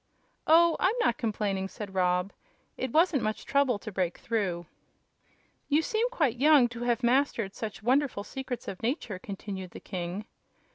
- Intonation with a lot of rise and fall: Yes, wide, 6.2 semitones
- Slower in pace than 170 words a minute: Yes, average, 155 wpm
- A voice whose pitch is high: Yes, high, 230 Hz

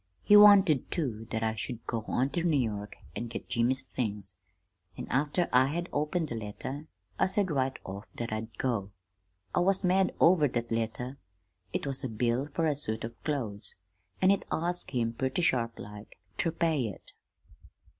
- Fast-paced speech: No, average, 175 wpm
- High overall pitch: No, low, 130 Hz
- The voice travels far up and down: Yes, wide, 6.1 semitones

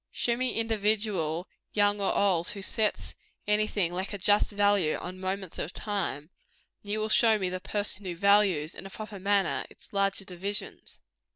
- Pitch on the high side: Yes, high, 200 Hz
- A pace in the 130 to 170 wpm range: No, average, 185 wpm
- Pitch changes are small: Yes, narrow, 2.1 semitones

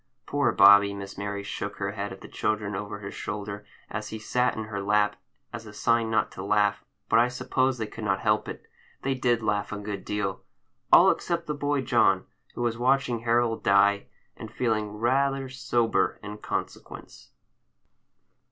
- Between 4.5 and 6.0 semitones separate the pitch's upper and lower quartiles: No, average, 3.0 semitones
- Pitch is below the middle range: Yes, low, 110 Hz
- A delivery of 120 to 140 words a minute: No, average, 175 wpm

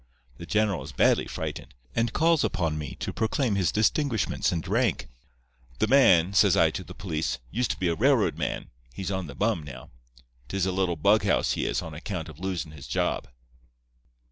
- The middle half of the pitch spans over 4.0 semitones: Yes, average, 4.8 semitones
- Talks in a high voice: No, very low, 95 Hz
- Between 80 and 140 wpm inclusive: No, average, 190 wpm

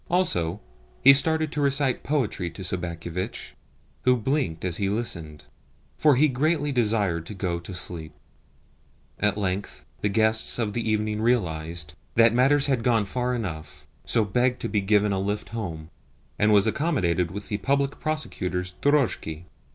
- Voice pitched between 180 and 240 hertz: No, low, 105 Hz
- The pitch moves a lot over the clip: Yes, wide, 6.0 semitones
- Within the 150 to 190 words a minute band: Yes, average, 155 wpm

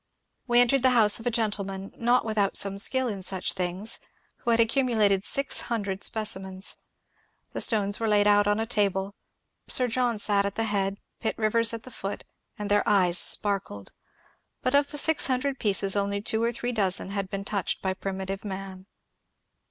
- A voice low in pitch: No, high, 205 Hz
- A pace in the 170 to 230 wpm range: Yes, average, 185 wpm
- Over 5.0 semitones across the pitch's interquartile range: No, average, 3.0 semitones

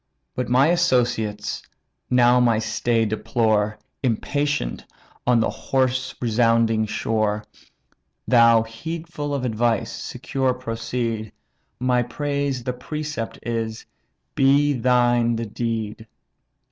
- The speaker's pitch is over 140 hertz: No, low, 120 Hz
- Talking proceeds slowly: Yes, slow, 100 wpm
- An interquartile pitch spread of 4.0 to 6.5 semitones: No, narrow, 2.4 semitones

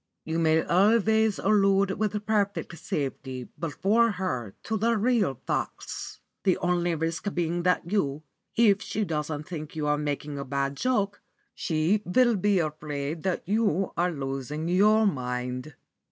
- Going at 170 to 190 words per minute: No, average, 140 wpm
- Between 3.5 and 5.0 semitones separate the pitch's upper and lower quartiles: No, wide, 5.5 semitones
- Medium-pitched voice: Yes, medium, 175 Hz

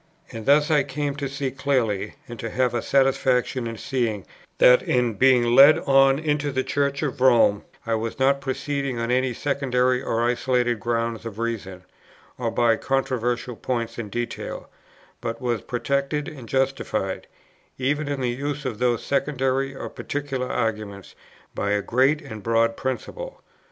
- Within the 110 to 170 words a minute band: Yes, average, 160 wpm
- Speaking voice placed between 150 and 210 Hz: No, low, 125 Hz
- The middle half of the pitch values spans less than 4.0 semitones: Yes, average, 3.0 semitones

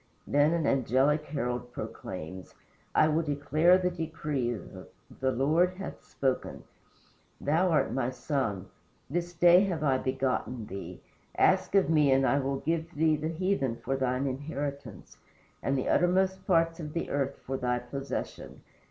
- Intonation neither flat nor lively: Yes, average, 4.1 semitones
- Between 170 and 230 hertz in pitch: No, medium, 145 Hz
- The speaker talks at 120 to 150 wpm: Yes, average, 145 wpm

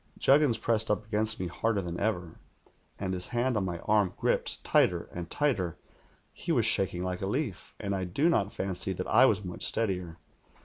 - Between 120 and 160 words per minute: No, average, 190 wpm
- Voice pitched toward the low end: Yes, low, 100 Hz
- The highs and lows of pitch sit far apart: No, average, 3.6 semitones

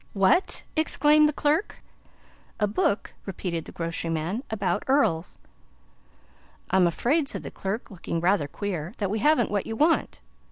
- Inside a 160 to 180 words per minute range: No, average, 150 wpm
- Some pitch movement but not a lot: No, wide, 8.0 semitones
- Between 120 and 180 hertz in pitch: No, high, 205 Hz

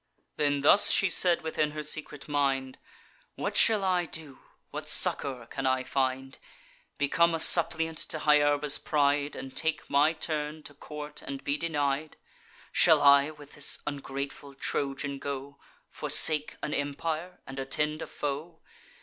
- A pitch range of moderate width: No, narrow, 2.0 semitones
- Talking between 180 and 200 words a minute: No, average, 145 wpm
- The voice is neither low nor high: Yes, medium, 145 Hz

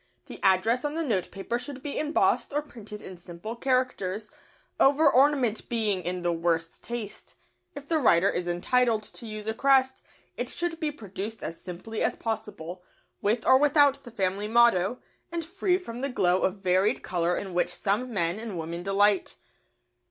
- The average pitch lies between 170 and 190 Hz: No, high, 220 Hz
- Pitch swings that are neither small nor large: No, wide, 6.0 semitones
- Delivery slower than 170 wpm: No, average, 175 wpm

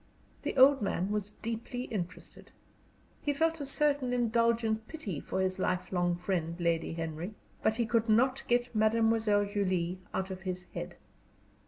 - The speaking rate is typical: Yes, average, 150 wpm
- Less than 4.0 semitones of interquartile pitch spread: No, average, 4.6 semitones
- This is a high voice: Yes, high, 215 Hz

